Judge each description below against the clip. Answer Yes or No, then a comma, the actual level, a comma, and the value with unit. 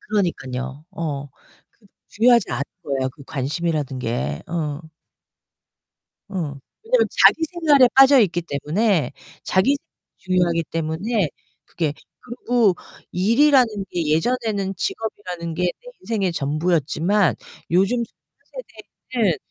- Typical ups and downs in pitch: No, wide, 6.8 semitones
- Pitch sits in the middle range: Yes, medium, 180 Hz